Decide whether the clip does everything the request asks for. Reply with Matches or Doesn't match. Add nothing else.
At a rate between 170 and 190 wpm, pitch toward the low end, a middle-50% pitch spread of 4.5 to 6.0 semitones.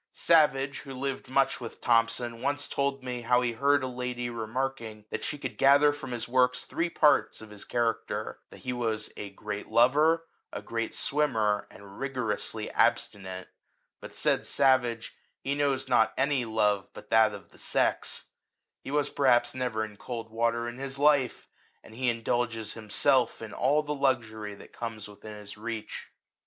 Doesn't match